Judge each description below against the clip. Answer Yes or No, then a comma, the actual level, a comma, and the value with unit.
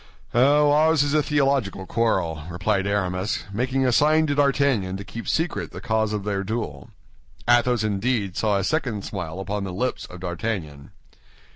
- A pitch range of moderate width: No, wide, 5.9 semitones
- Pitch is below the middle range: Yes, low, 110 Hz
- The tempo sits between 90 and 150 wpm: No, average, 165 wpm